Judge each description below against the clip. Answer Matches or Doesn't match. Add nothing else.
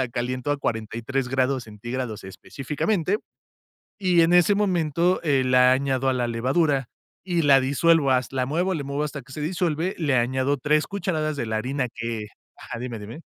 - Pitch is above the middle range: Doesn't match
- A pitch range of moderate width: Matches